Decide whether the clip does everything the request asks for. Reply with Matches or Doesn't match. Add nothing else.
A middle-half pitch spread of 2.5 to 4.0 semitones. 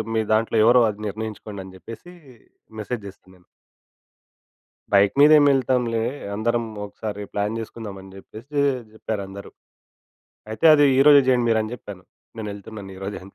Matches